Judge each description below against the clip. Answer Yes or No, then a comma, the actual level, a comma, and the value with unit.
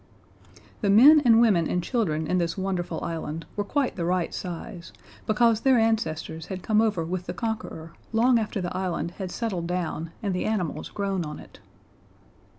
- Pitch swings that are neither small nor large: Yes, average, 4.5 semitones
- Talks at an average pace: Yes, average, 175 wpm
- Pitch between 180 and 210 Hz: Yes, medium, 185 Hz